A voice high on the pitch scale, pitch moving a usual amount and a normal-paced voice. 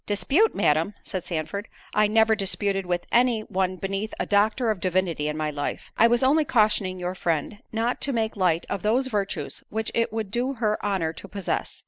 Yes: high, 205 Hz; average, 3.4 semitones; average, 195 wpm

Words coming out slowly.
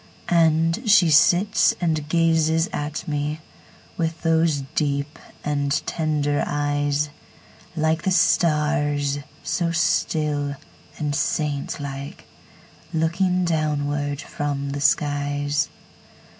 Yes: slow, 85 wpm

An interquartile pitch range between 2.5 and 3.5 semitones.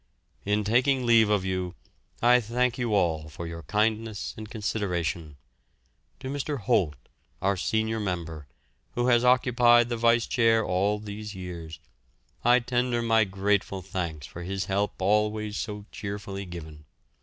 No: average, 4.1 semitones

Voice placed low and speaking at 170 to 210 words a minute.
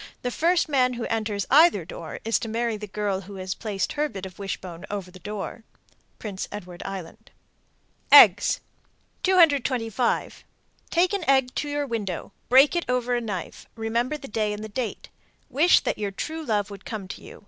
No: high, 225 Hz; average, 180 wpm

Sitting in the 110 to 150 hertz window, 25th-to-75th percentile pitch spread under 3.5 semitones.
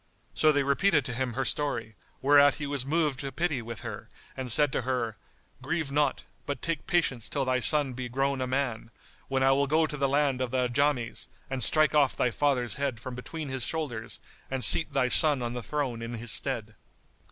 Yes: low, 135 Hz; average, 2.7 semitones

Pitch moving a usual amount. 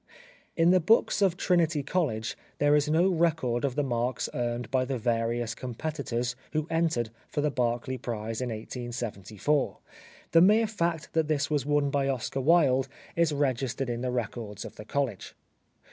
Yes: average, 4.8 semitones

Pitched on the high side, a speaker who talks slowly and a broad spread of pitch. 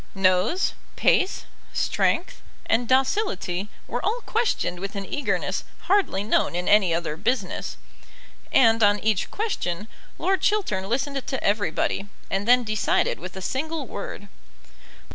Yes: high, 215 Hz; slow, 130 wpm; wide, 6.5 semitones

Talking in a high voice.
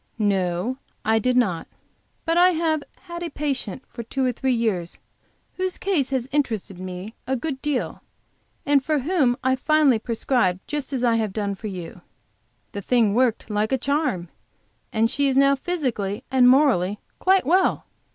Yes: very high, 255 Hz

